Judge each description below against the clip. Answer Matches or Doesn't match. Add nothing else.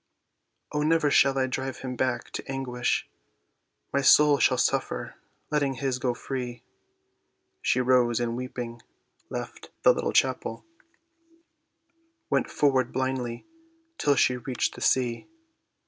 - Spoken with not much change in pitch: Matches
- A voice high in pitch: Doesn't match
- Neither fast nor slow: Doesn't match